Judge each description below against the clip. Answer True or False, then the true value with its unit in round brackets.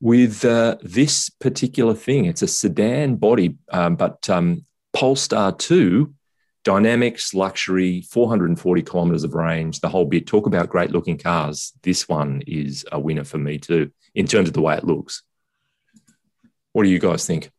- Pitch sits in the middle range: False (100 Hz)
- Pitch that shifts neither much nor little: False (7.9 semitones)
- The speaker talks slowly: False (165 wpm)